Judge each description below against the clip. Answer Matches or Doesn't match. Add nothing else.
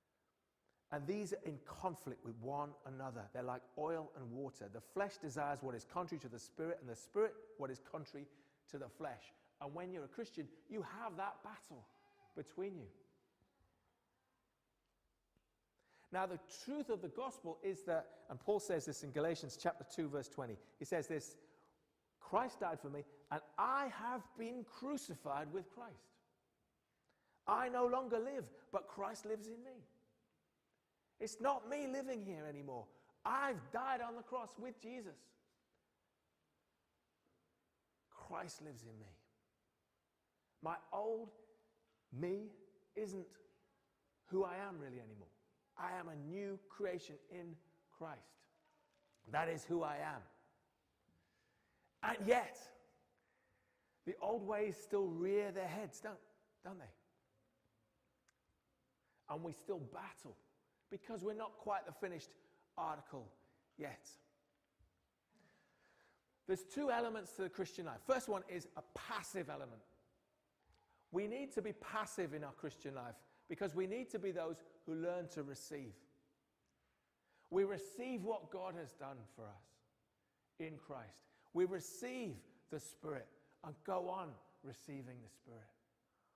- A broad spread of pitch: Matches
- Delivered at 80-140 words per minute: Matches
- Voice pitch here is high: Doesn't match